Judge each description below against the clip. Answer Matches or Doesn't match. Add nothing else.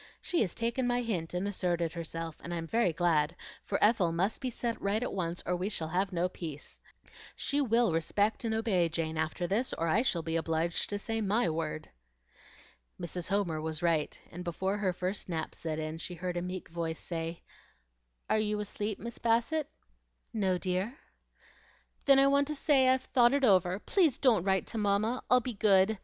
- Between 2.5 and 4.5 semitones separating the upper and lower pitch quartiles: Doesn't match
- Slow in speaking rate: Doesn't match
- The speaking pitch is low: Doesn't match